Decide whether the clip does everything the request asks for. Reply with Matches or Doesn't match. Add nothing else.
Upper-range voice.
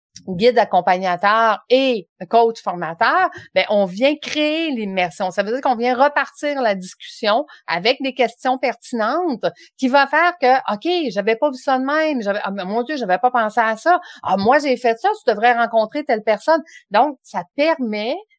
Matches